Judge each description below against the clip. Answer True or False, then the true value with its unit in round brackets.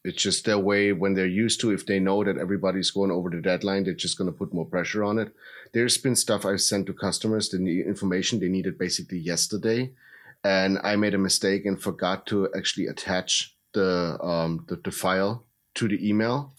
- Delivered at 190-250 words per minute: True (205 wpm)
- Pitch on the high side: False (100 Hz)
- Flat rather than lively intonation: True (2.1 semitones)